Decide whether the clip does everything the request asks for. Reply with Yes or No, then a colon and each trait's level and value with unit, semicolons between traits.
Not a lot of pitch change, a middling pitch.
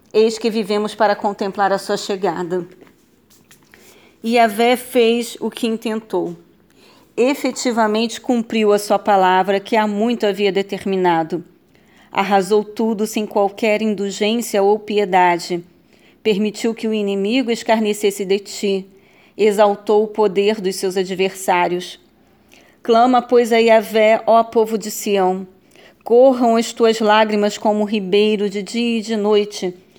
No: narrow, 2.2 semitones; high, 210 Hz